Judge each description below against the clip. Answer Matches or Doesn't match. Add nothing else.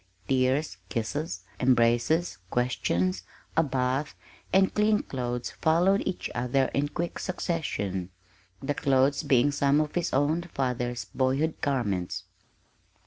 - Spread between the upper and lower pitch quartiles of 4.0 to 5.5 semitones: Matches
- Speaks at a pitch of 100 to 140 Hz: Matches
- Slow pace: Matches